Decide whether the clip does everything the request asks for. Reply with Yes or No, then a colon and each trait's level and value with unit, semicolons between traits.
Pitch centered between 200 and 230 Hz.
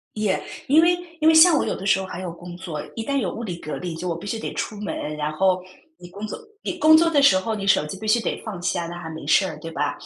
No: high, 190 Hz